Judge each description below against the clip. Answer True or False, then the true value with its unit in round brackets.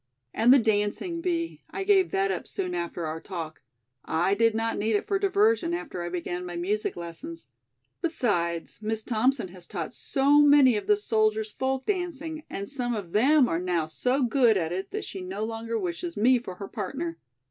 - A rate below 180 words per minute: False (190 wpm)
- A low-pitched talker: False (225 Hz)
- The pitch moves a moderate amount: False (8.2 semitones)